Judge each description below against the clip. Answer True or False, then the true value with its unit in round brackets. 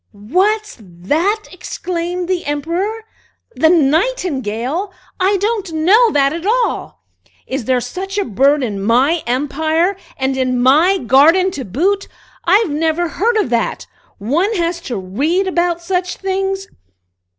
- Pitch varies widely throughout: True (6.2 semitones)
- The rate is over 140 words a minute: False (135 wpm)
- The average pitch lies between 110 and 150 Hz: False (335 Hz)